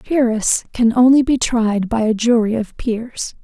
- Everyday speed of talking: Yes, average, 190 wpm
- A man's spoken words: No, female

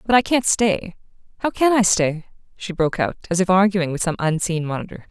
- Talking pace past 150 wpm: Yes, average, 200 wpm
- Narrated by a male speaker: No, female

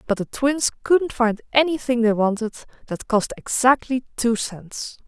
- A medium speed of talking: Yes, average, 155 wpm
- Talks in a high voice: Yes, high, 240 Hz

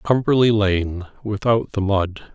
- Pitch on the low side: Yes, low, 105 Hz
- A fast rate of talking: No, slow, 130 wpm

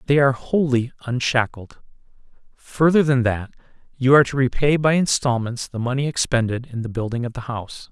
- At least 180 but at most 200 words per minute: No, average, 165 wpm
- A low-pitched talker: Yes, low, 130 Hz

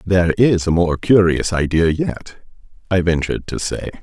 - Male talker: Yes, male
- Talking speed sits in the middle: Yes, average, 165 wpm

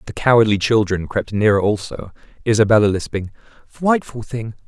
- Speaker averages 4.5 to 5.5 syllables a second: Yes, 5.4 syllables/s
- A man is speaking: Yes, male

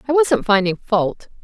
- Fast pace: No, average, 165 wpm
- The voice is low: No, high, 225 Hz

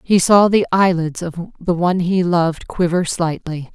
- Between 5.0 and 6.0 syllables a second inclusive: No, 4.8 syllables/s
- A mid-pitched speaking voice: Yes, medium, 175 Hz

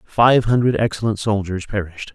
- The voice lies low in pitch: Yes, low, 110 Hz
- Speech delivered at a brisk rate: No, average, 140 wpm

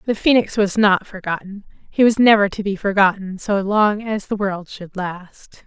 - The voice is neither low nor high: No, high, 200 Hz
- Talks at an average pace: Yes, average, 190 wpm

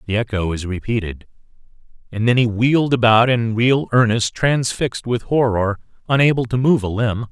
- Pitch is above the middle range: No, low, 115 Hz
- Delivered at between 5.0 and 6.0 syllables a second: Yes, 5.2 syllables/s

